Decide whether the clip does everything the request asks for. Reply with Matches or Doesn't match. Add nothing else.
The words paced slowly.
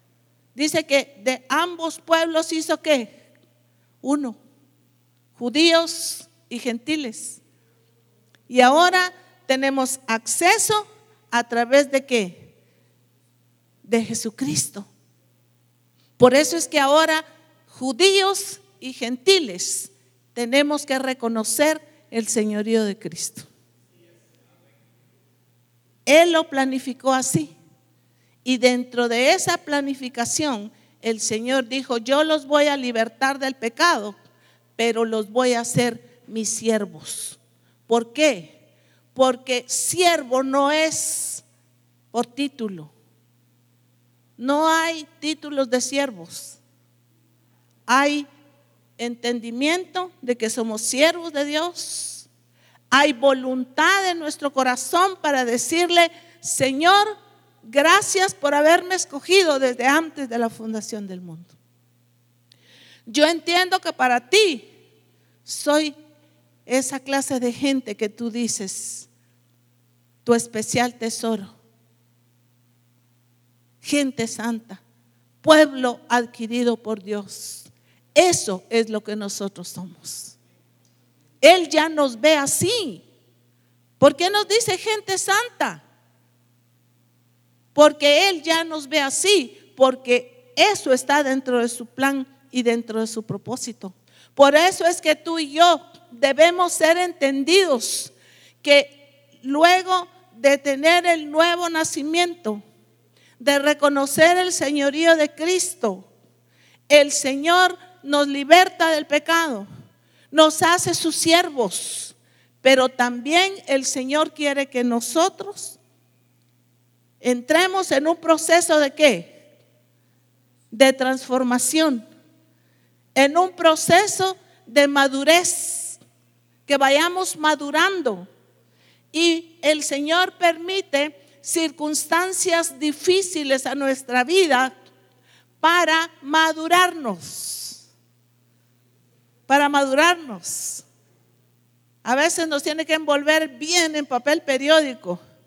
Matches